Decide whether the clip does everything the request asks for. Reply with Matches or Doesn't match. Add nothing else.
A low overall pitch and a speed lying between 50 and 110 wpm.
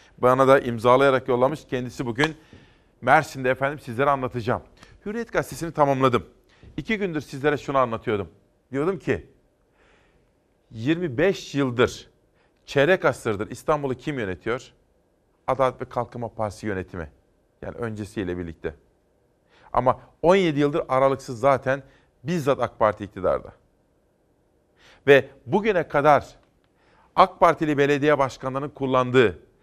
Matches